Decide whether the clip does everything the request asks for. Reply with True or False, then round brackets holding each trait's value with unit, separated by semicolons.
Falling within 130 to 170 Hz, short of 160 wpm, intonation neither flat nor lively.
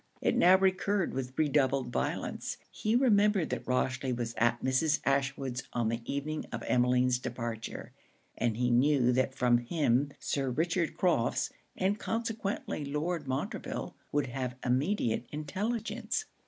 False (140 Hz; 135 wpm; 6.0 semitones)